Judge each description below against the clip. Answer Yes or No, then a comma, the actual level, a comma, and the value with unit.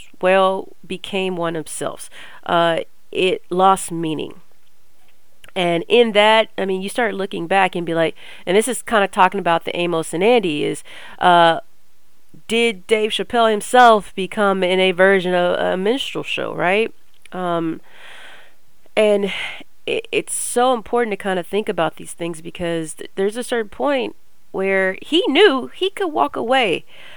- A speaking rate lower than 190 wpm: Yes, average, 160 wpm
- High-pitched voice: Yes, high, 195 Hz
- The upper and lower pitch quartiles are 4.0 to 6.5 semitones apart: Yes, average, 4.7 semitones